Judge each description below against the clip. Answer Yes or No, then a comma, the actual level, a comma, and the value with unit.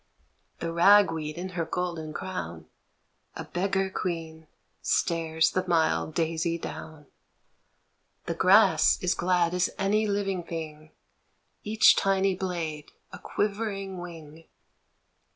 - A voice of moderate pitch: Yes, medium, 170 Hz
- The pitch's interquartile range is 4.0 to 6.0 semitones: No, average, 3.0 semitones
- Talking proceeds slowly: Yes, slow, 115 wpm